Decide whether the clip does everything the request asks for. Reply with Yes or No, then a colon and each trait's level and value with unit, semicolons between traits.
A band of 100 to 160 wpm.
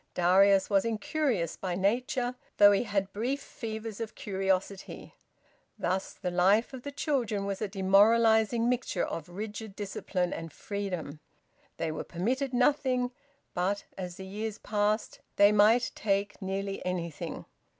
Yes: average, 140 wpm